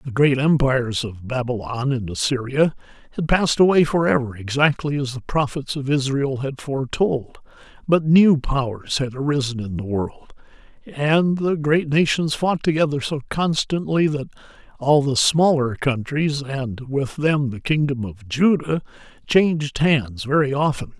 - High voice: No, medium, 140 Hz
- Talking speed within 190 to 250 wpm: No, average, 150 wpm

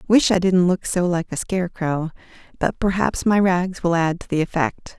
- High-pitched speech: No, medium, 175 Hz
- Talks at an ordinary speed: No, fast, 215 wpm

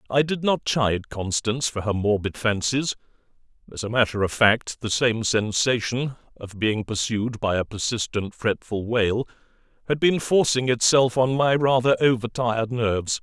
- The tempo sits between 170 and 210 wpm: No, average, 160 wpm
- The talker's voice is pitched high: No, low, 115 Hz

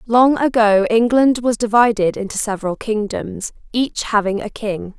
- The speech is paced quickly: No, average, 145 wpm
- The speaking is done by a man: No, female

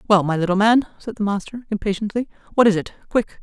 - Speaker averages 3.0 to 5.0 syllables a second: No, 6.6 syllables/s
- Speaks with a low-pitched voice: No, high, 210 Hz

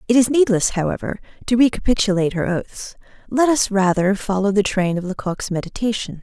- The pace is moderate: Yes, average, 165 wpm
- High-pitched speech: Yes, high, 205 Hz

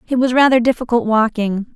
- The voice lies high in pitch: Yes, high, 235 Hz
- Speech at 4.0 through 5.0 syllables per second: No, 5.9 syllables/s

